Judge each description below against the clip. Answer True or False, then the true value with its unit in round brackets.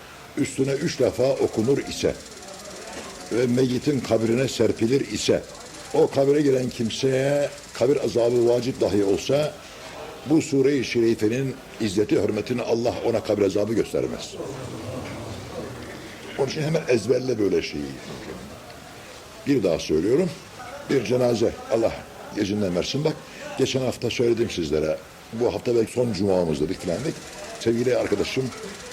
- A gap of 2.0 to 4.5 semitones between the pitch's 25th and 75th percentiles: True (3.8 semitones)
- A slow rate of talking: False (115 wpm)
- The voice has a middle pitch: False (120 Hz)